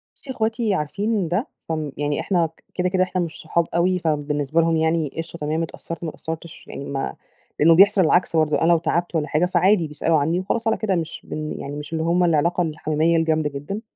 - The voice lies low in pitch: No, medium, 165 Hz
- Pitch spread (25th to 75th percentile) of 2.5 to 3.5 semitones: Yes, average, 2.8 semitones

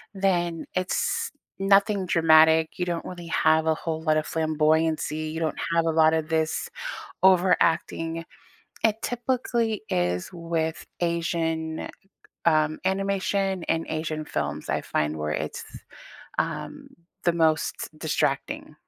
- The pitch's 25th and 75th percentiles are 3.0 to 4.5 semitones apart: No, narrow, 2.5 semitones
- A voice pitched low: No, medium, 165 Hz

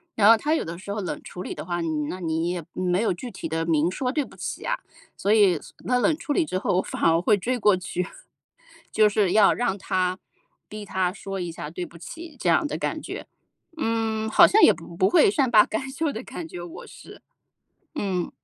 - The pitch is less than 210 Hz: Yes, high, 195 Hz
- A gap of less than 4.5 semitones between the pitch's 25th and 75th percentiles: No, average, 5.3 semitones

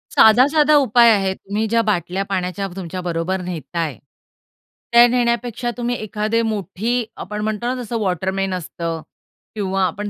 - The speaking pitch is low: No, high, 205 Hz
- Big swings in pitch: No, average, 4.2 semitones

